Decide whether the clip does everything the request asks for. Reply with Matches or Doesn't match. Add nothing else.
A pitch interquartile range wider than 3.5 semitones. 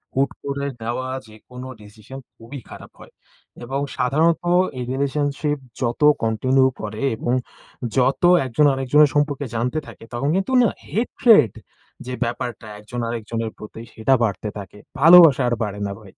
Matches